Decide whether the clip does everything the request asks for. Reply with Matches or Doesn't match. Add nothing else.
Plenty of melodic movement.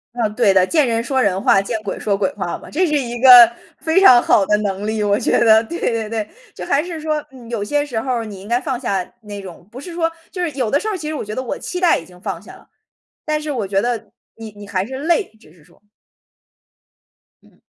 Matches